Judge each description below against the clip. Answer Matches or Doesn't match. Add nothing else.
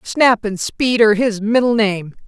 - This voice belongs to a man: Doesn't match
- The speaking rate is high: Doesn't match